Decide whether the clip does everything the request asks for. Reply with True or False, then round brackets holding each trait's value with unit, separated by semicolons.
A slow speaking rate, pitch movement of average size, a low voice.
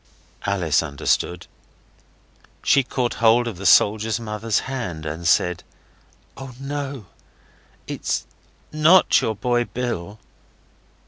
False (105 wpm; 6.2 semitones; 110 Hz)